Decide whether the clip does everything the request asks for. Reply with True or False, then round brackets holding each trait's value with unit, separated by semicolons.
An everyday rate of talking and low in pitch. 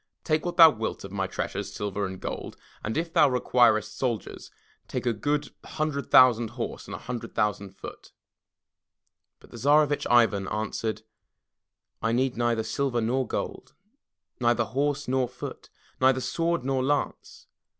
True (150 wpm; 120 Hz)